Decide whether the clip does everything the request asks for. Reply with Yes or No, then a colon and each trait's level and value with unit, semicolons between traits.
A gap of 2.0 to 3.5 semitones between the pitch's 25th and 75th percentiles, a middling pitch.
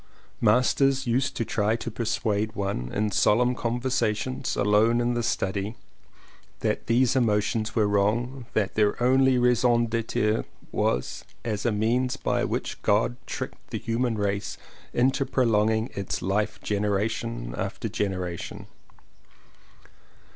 No: average, 2.8 semitones; low, 115 Hz